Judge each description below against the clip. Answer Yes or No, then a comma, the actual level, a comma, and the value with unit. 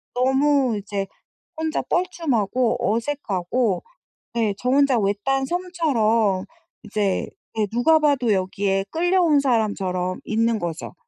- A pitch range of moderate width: No, wide, 5.9 semitones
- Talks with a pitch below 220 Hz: No, high, 230 Hz